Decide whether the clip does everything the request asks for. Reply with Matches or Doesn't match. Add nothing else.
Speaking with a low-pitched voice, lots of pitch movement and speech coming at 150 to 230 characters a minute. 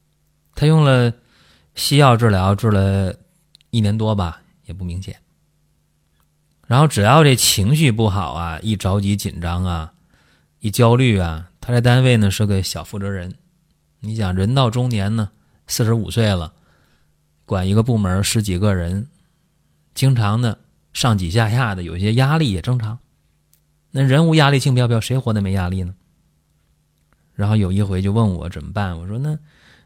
Matches